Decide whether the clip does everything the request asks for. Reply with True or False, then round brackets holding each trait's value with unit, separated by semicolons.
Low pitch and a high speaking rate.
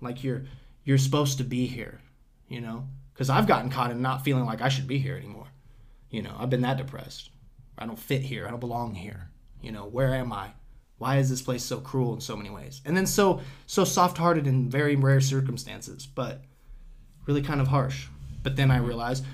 True (130 Hz; 215 wpm)